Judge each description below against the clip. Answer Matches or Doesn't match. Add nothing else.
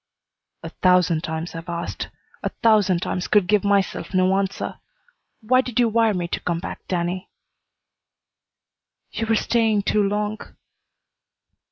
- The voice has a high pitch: Matches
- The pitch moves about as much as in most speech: Matches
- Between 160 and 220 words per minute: Doesn't match